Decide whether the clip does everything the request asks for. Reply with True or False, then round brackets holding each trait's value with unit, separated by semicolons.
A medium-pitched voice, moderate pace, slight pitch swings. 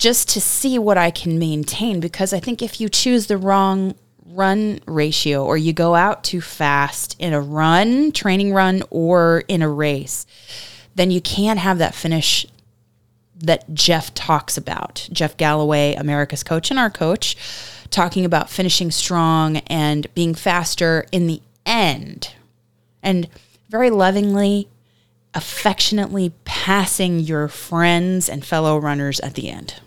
False (170 Hz; 145 wpm; 4.3 semitones)